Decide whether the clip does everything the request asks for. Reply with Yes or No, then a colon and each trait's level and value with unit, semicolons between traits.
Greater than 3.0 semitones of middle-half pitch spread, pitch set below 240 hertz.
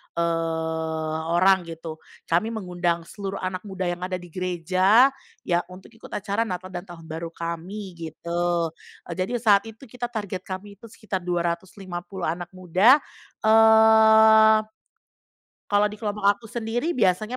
Yes: average, 4.0 semitones; medium, 185 Hz